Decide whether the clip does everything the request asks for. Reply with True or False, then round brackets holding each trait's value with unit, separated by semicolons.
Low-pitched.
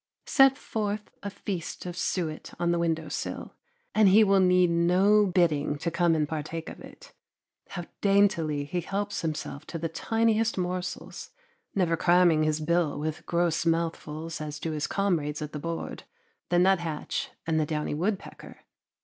False (170 Hz)